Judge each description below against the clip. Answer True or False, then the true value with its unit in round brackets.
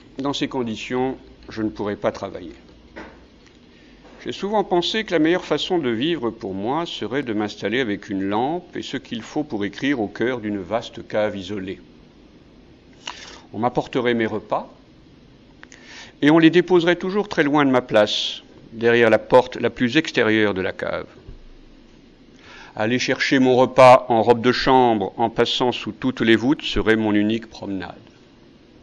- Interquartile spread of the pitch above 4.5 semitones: True (5.0 semitones)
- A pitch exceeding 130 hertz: False (120 Hz)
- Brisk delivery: False (160 wpm)